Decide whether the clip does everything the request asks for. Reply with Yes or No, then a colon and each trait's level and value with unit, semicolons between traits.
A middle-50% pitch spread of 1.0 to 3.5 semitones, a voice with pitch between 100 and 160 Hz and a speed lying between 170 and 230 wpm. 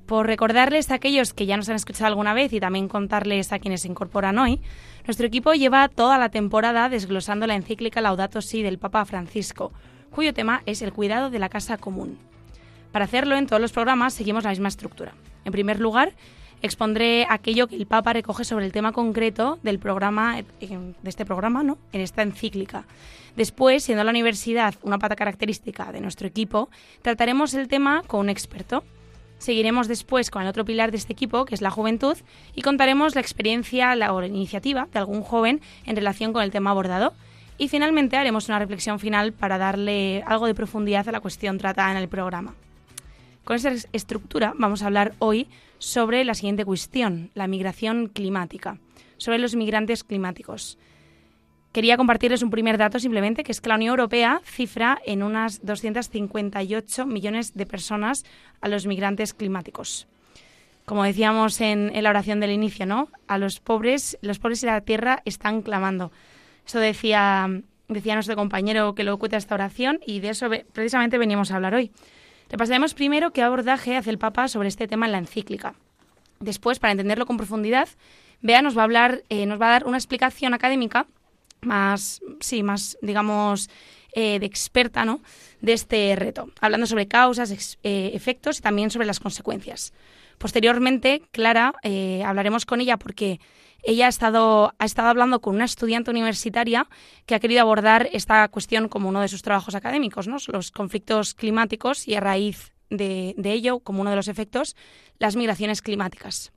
No: average, 2.9 semitones; high, 220 Hz; average, 180 wpm